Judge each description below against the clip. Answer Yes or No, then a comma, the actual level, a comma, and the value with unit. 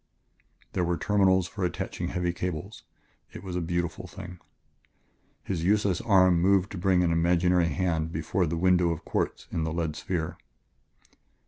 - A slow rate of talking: No, average, 155 wpm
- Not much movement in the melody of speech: Yes, narrow, 1.8 semitones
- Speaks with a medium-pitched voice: No, very low, 90 Hz